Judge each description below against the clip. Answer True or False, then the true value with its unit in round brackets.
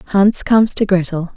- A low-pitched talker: False (195 Hz)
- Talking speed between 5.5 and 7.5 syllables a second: False (4.7 syllables/s)